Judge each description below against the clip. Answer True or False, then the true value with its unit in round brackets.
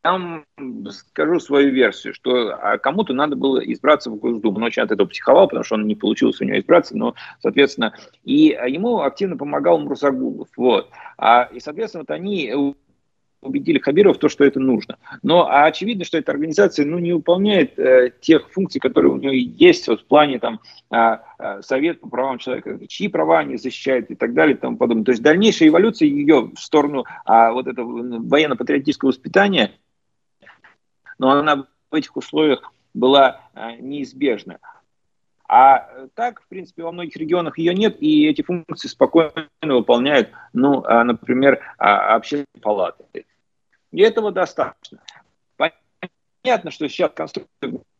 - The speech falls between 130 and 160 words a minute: True (150 wpm)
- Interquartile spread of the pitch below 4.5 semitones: False (5.5 semitones)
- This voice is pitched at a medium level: True (150 Hz)